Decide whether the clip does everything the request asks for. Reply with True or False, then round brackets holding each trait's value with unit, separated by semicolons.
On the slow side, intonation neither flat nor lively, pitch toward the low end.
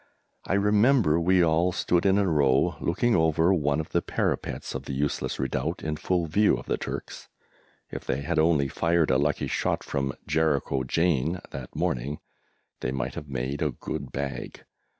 False (175 wpm; 4.1 semitones; 75 Hz)